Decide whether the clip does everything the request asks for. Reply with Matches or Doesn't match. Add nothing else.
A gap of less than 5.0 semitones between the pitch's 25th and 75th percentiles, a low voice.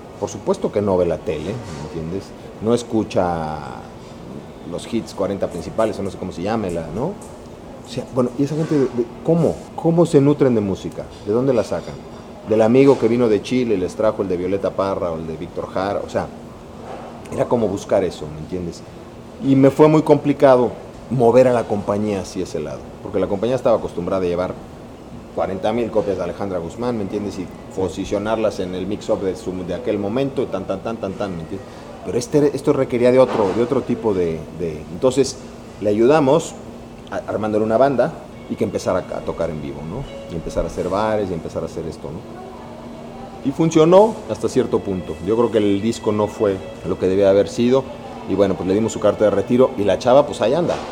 Doesn't match